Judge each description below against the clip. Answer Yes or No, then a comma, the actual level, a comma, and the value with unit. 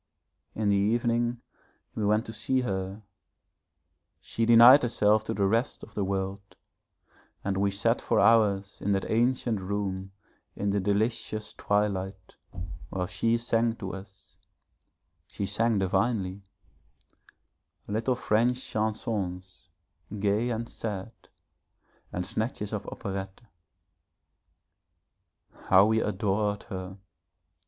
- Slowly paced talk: Yes, slow, 115 wpm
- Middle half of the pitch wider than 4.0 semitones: No, average, 2.8 semitones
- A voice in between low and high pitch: No, low, 105 Hz